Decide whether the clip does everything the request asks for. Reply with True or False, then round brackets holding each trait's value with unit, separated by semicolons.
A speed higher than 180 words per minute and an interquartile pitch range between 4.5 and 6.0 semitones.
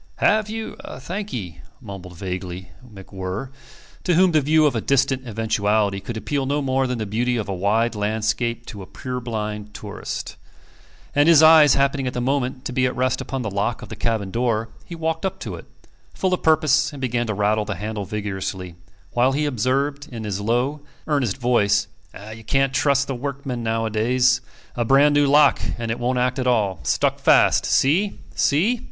True (190 wpm; 4.8 semitones)